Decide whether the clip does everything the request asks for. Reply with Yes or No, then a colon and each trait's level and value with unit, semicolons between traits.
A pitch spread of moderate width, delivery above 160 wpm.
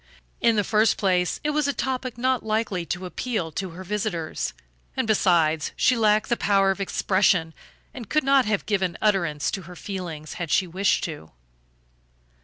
Yes: average, 4.0 semitones; average, 175 wpm